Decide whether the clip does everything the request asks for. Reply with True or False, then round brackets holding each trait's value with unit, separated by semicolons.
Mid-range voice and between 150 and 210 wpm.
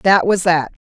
True (175 Hz; 205 wpm)